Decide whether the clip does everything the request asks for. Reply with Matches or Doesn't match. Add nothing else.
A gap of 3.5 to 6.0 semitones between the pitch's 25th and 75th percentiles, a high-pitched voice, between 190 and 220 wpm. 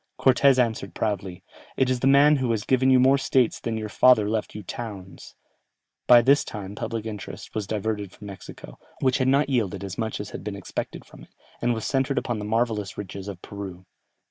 Doesn't match